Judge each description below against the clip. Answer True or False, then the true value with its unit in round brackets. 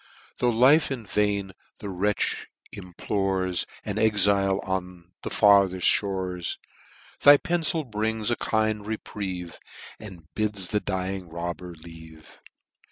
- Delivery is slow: True (115 wpm)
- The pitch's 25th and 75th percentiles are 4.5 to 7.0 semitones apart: False (2.9 semitones)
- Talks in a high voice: False (100 Hz)